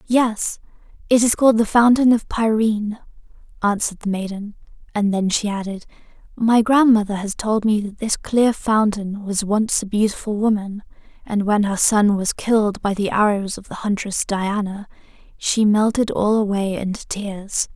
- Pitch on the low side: No, high, 210 Hz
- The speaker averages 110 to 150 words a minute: No, average, 160 wpm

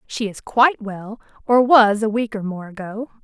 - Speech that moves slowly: No, fast, 205 wpm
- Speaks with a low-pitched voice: No, high, 220 Hz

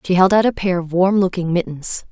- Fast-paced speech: Yes, fast, 255 wpm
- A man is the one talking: No, female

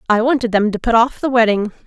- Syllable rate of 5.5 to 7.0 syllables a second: Yes, 6.3 syllables/s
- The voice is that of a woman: Yes, female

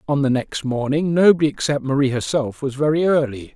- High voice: No, medium, 140 Hz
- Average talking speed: Yes, average, 185 wpm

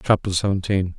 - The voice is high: No, very low, 95 Hz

